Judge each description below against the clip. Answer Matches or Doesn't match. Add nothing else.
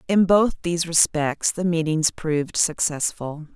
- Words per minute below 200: Matches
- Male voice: Doesn't match